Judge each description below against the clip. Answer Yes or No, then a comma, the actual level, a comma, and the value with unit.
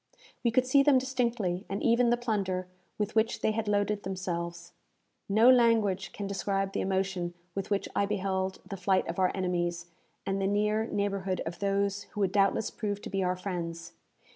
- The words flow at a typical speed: Yes, average, 185 wpm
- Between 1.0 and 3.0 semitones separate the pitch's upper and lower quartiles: Yes, narrow, 2.4 semitones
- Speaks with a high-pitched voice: Yes, high, 195 Hz